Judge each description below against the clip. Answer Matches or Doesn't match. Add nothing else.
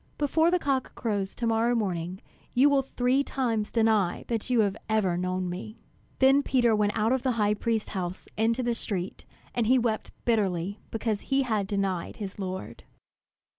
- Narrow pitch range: Doesn't match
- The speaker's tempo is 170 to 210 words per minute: Matches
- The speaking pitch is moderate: Doesn't match